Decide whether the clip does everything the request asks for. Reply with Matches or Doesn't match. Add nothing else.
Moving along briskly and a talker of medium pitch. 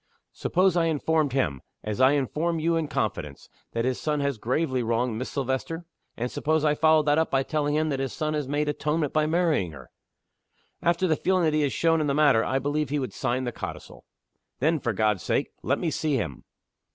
Matches